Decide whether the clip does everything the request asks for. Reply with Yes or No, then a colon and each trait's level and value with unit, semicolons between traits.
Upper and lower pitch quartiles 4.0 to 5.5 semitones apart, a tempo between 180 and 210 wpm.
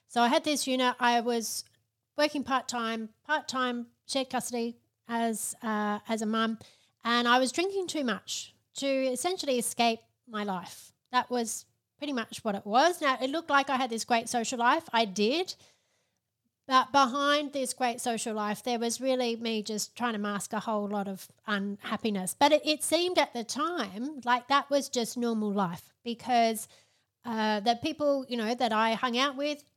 No: average, 3.3 semitones; average, 185 wpm